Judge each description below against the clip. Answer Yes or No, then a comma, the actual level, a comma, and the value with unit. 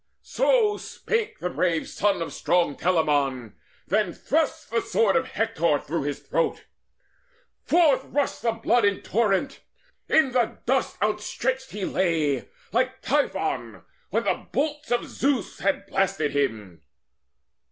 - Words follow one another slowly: Yes, slow, 130 wpm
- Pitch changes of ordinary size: No, wide, 8.0 semitones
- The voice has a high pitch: Yes, high, 210 Hz